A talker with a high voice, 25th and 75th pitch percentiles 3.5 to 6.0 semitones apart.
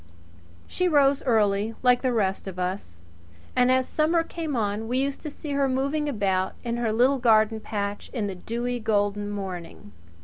Yes: high, 230 Hz; average, 4.8 semitones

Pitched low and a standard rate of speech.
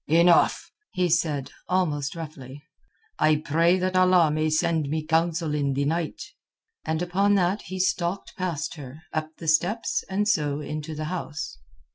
No: medium, 160 Hz; average, 155 wpm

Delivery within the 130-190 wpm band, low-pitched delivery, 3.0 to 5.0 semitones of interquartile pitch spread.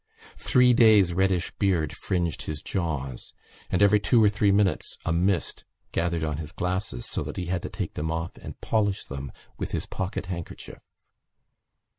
Yes: average, 170 wpm; very low, 90 Hz; average, 3.6 semitones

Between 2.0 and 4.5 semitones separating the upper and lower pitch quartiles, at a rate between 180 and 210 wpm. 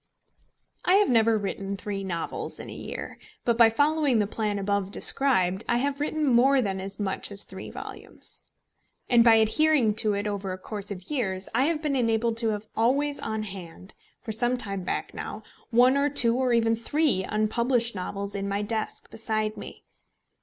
Yes: average, 3.9 semitones; average, 185 wpm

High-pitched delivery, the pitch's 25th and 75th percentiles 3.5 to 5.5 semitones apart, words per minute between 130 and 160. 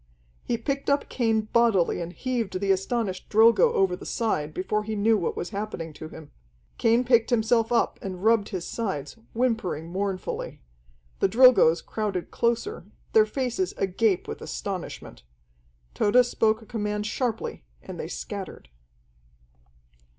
Yes: high, 215 Hz; average, 4.1 semitones; average, 145 wpm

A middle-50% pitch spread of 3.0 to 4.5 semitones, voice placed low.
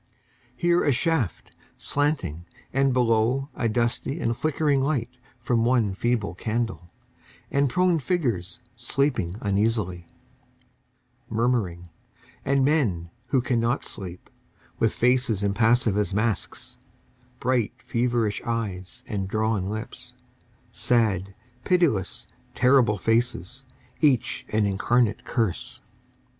Yes: average, 4.2 semitones; low, 115 Hz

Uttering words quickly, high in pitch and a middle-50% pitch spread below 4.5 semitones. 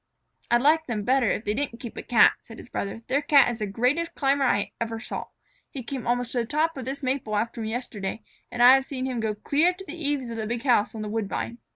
Yes: fast, 260 wpm; high, 245 Hz; average, 3.6 semitones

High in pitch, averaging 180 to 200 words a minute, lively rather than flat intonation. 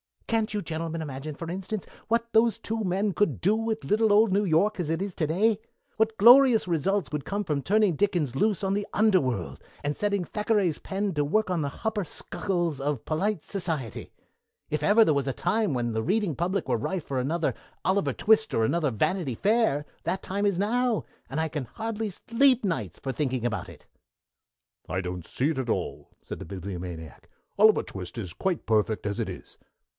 No: medium, 180 Hz; average, 195 wpm; wide, 6.8 semitones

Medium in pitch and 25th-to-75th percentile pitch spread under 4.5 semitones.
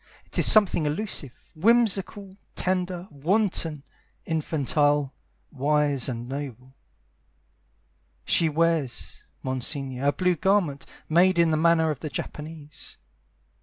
Yes: medium, 155 Hz; average, 4.1 semitones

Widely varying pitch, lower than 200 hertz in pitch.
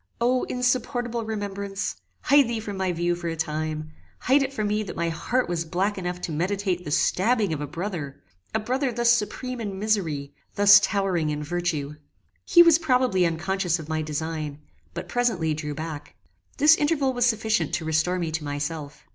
Yes: wide, 6.5 semitones; medium, 185 Hz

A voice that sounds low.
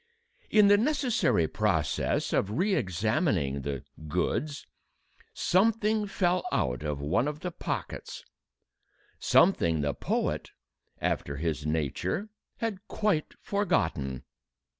Yes: low, 110 Hz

